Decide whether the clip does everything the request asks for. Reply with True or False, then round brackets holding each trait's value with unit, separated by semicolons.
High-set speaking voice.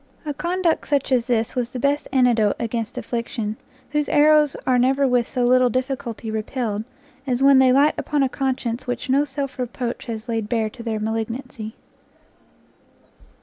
True (250 Hz)